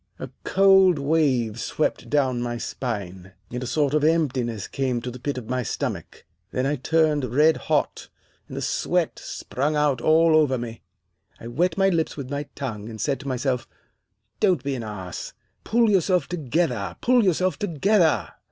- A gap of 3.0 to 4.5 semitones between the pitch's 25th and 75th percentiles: No, average, 5.0 semitones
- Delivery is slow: No, average, 170 wpm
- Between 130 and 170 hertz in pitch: Yes, medium, 140 Hz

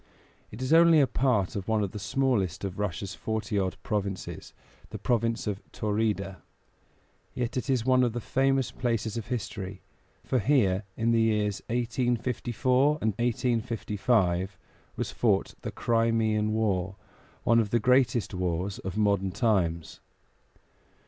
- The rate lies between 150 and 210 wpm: No, average, 140 wpm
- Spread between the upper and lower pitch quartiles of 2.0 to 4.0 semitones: Yes, average, 3.7 semitones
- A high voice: No, low, 110 Hz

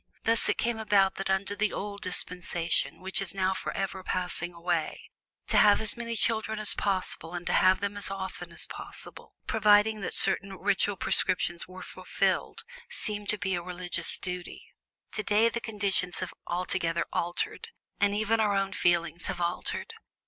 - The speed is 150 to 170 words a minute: Yes, average, 165 wpm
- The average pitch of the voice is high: Yes, high, 195 Hz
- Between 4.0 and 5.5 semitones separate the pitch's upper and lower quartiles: No, average, 2.7 semitones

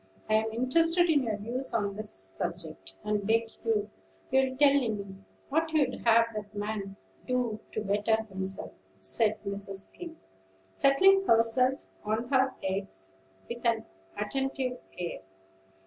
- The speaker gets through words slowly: Yes, slow, 130 wpm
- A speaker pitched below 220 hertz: No, high, 225 Hz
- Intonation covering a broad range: No, average, 4.3 semitones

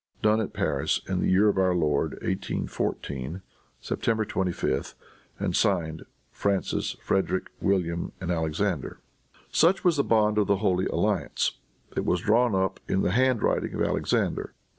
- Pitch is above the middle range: No, very low, 95 Hz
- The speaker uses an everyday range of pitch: Yes, average, 3.5 semitones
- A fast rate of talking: No, average, 150 wpm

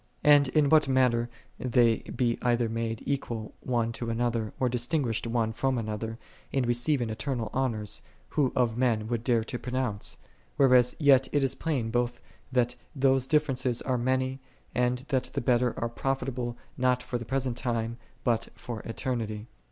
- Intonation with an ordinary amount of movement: No, narrow, 2.1 semitones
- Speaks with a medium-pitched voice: No, low, 125 Hz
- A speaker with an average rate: Yes, average, 165 wpm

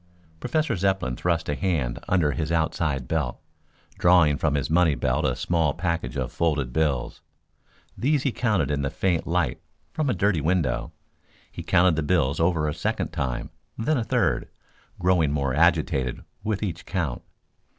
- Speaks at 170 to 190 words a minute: No, average, 160 wpm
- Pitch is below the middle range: Yes, very low, 80 Hz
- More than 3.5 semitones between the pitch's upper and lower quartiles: Yes, average, 4.2 semitones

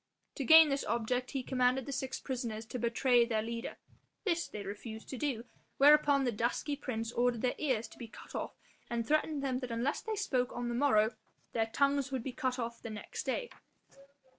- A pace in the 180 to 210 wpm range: Yes, average, 200 wpm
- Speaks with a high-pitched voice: Yes, very high, 250 Hz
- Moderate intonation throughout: Yes, average, 3.1 semitones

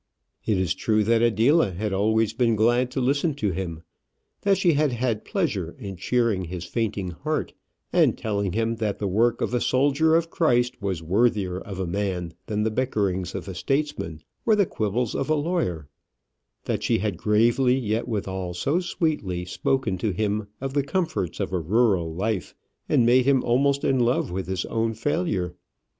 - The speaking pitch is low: Yes, low, 110 Hz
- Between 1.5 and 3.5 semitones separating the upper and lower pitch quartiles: No, average, 5.3 semitones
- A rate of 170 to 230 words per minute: Yes, average, 180 wpm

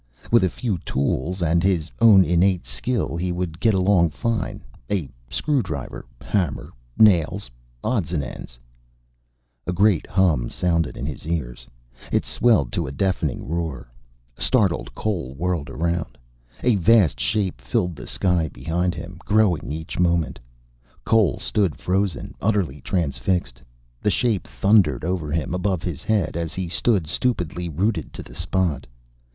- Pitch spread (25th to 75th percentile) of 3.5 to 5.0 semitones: Yes, average, 4.1 semitones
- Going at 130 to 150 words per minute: Yes, average, 145 wpm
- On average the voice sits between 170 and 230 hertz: No, very low, 90 Hz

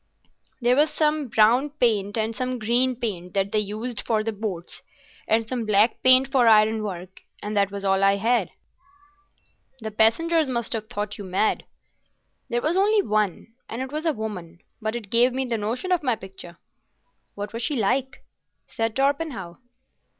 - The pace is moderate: Yes, average, 170 wpm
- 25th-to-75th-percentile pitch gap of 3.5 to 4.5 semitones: Yes, average, 3.9 semitones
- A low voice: No, high, 225 Hz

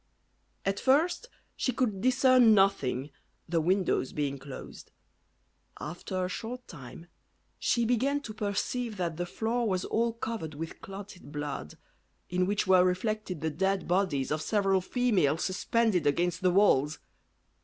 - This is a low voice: No, high, 190 Hz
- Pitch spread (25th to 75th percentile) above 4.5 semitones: Yes, wide, 5.4 semitones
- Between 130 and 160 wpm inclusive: Yes, average, 140 wpm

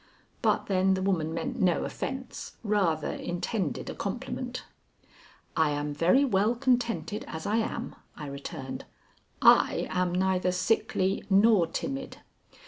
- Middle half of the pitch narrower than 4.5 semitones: No, average, 5.2 semitones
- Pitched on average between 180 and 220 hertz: Yes, high, 190 Hz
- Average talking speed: No, slow, 130 wpm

